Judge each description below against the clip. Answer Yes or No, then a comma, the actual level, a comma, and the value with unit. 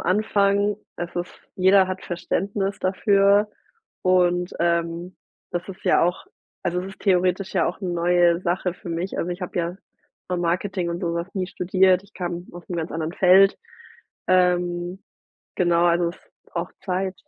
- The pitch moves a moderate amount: No, narrow, 1.6 semitones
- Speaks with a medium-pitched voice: Yes, medium, 180 Hz